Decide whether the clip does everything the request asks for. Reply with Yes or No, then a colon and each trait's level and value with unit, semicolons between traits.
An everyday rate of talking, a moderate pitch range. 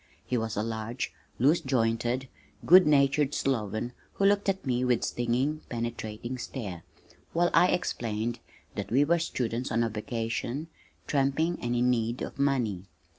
Yes: average, 150 wpm; average, 3.7 semitones